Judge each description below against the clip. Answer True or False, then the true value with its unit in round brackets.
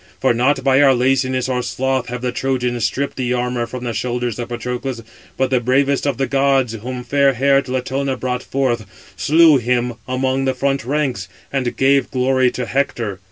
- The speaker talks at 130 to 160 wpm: False (185 wpm)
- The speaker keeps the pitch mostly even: True (1.7 semitones)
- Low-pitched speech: True (130 Hz)